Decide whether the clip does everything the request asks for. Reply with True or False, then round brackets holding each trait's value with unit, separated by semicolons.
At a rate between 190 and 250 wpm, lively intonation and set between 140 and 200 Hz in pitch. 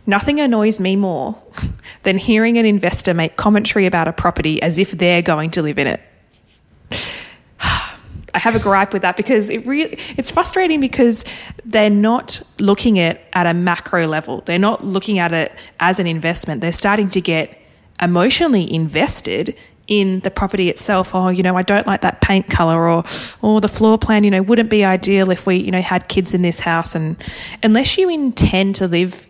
False (195 wpm; 3.5 semitones; 190 Hz)